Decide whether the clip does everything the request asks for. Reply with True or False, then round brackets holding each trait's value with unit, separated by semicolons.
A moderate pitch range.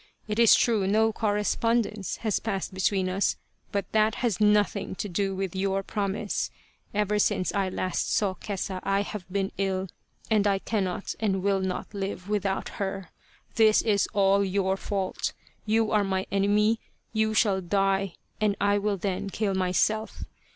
False (1.7 semitones)